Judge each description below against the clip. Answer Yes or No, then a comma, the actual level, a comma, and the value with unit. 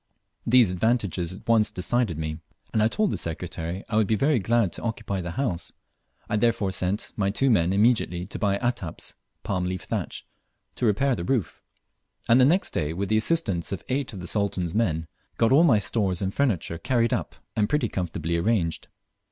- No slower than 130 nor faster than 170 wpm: No, average, 195 wpm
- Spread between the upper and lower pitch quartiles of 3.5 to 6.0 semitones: Yes, average, 4.7 semitones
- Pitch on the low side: Yes, low, 105 Hz